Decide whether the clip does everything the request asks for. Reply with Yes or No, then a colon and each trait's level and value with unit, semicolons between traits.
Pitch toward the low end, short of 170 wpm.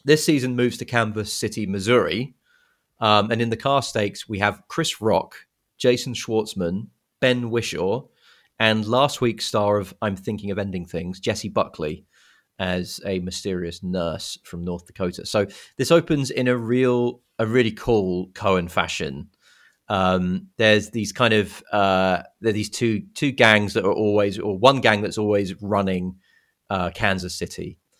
Yes: low, 105 Hz; average, 160 wpm